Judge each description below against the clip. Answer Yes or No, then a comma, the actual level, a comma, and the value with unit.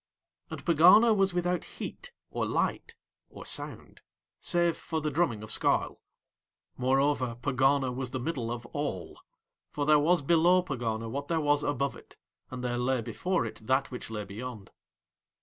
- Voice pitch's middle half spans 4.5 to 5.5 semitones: Yes, average, 5.1 semitones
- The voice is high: No, medium, 140 Hz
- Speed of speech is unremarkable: Yes, average, 160 wpm